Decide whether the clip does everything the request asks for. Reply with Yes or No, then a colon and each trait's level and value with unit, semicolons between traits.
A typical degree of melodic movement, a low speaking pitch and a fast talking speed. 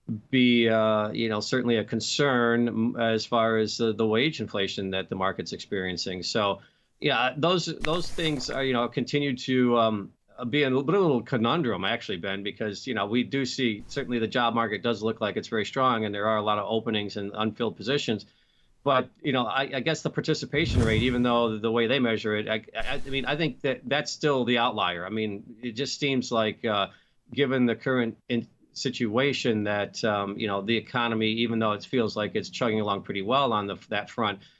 Yes: average, 3.3 semitones; low, 115 Hz; fast, 210 wpm